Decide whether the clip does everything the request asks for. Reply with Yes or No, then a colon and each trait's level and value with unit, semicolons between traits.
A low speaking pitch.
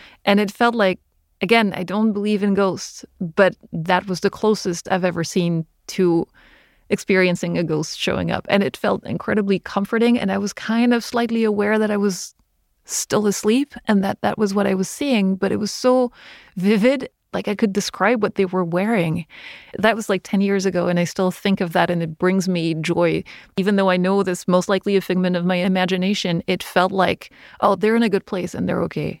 No: high, 195 Hz